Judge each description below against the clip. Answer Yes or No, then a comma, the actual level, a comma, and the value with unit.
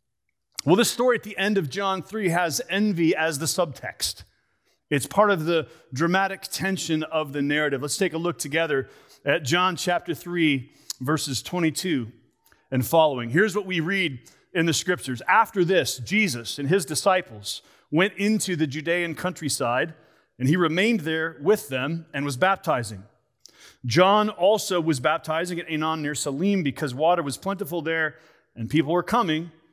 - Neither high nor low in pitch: Yes, medium, 165 Hz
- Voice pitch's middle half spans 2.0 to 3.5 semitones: No, average, 4.2 semitones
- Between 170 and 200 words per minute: No, average, 160 wpm